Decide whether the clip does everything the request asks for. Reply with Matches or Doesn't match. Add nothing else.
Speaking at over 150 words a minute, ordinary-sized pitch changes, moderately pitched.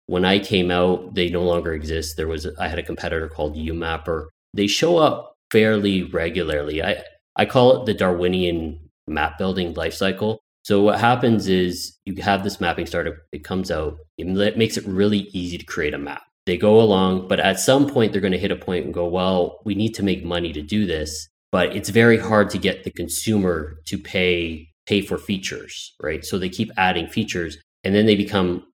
Doesn't match